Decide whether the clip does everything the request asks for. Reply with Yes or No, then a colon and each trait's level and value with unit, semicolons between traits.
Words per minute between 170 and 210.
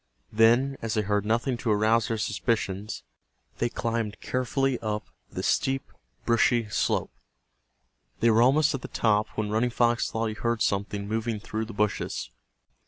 No: average, 160 wpm